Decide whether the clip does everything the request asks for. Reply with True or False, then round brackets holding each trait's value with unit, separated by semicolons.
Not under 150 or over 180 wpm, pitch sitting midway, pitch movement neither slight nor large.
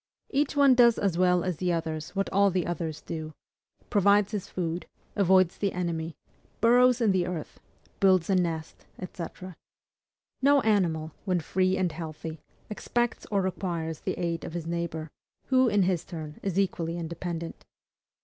True (160 wpm; 180 Hz; 3.3 semitones)